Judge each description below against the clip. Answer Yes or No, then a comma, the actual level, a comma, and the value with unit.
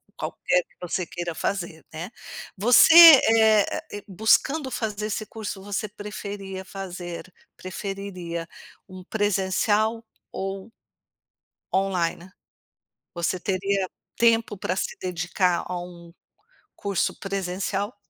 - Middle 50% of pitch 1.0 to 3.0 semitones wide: Yes, average, 2.7 semitones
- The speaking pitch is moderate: No, high, 195 Hz